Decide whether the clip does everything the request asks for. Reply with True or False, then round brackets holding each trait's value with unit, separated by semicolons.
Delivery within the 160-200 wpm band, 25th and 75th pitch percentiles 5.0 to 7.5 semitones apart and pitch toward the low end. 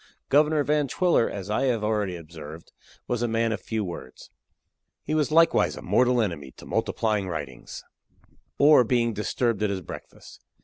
True (165 wpm; 5.5 semitones; 110 Hz)